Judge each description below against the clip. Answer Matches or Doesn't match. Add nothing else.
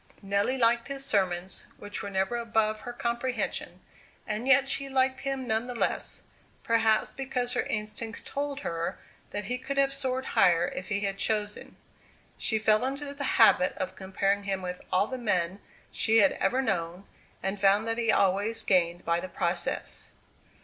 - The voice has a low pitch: Doesn't match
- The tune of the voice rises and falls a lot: Doesn't match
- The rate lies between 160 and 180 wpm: Matches